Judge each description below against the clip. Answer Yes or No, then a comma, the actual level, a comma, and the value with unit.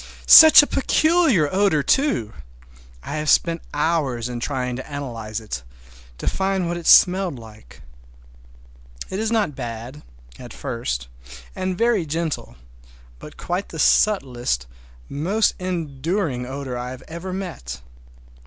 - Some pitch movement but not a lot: No, wide, 7.4 semitones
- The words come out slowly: Yes, slow, 125 wpm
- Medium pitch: Yes, medium, 150 Hz